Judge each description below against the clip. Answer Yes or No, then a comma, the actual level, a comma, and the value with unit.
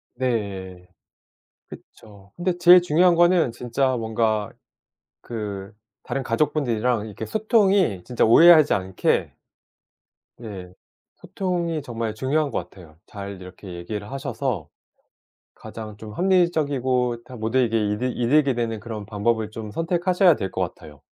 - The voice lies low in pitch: Yes, low, 115 Hz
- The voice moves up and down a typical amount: No, wide, 6.5 semitones